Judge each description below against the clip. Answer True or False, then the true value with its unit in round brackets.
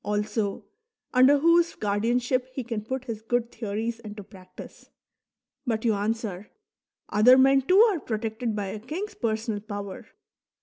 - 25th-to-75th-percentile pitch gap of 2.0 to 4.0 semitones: True (3.5 semitones)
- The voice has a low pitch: False (225 Hz)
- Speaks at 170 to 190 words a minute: False (145 wpm)